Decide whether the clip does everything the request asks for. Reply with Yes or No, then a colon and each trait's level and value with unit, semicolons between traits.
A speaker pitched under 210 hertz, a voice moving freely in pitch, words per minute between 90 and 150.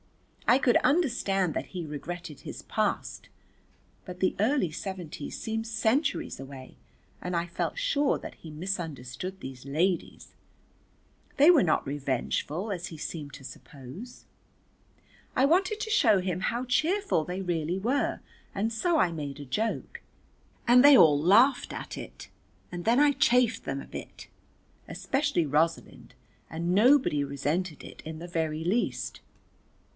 Yes: medium, 185 Hz; wide, 7.9 semitones; average, 145 wpm